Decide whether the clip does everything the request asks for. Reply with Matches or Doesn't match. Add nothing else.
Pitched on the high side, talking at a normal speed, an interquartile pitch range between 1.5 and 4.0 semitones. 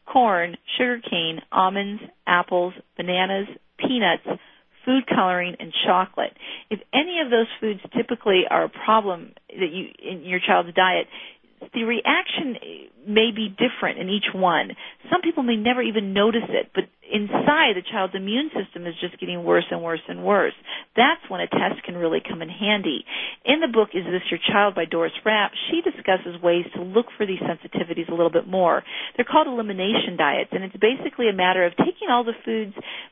Doesn't match